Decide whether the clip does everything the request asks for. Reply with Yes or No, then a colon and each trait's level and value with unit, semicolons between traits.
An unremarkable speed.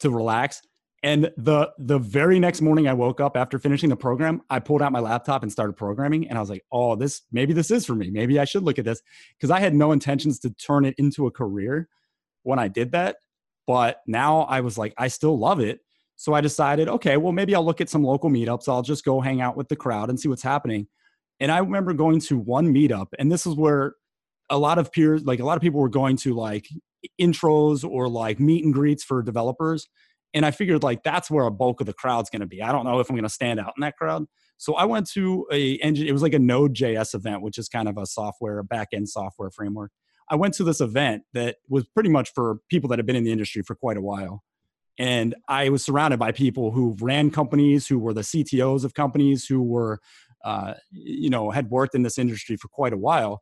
No: fast, 245 wpm